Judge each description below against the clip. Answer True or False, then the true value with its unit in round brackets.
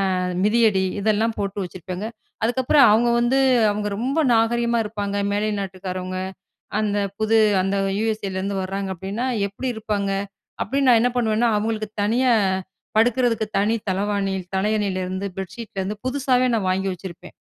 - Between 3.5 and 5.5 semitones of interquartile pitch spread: False (3.1 semitones)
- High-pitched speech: True (210 Hz)